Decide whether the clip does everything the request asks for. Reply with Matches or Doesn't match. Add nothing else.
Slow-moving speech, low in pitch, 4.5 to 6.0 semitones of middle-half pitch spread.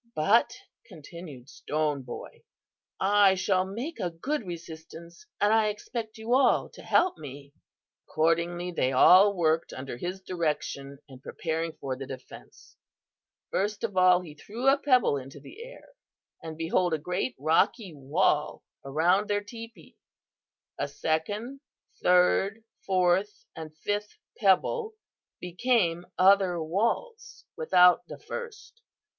Doesn't match